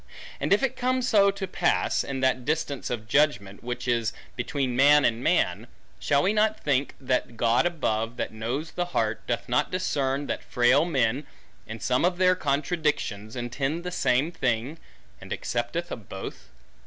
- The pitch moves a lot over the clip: Yes, wide, 5.8 semitones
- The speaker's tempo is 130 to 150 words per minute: No, average, 170 wpm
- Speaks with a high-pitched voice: No, low, 135 Hz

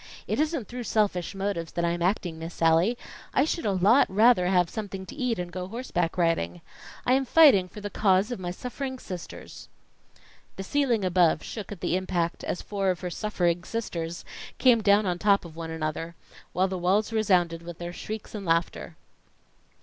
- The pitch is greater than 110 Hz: Yes, high, 190 Hz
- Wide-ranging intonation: No, average, 4.0 semitones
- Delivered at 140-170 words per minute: No, average, 190 wpm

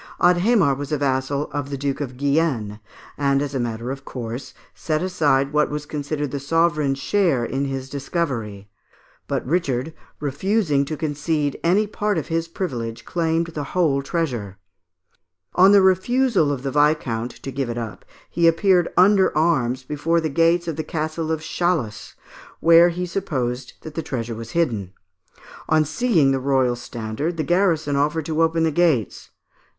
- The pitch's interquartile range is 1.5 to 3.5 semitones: No, average, 3.9 semitones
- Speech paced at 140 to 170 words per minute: Yes, average, 165 wpm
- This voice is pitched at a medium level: Yes, medium, 150 Hz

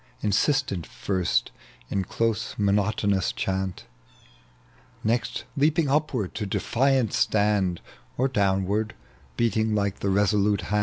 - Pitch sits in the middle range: No, low, 105 Hz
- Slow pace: Yes, slow, 105 wpm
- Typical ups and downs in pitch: Yes, average, 3.0 semitones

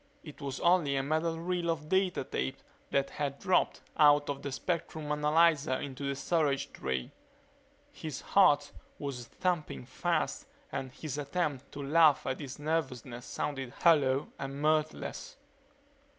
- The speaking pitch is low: No, medium, 145 Hz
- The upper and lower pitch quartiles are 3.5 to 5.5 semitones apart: No, average, 2.8 semitones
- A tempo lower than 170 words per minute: Yes, average, 140 wpm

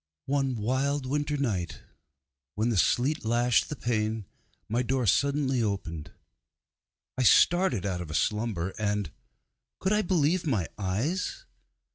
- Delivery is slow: Yes, slow, 130 wpm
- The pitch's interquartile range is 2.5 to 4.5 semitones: No, wide, 5.6 semitones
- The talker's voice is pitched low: Yes, low, 120 Hz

